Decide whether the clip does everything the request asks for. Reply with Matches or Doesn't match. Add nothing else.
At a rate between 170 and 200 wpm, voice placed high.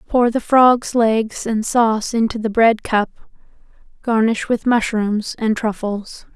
Doesn't match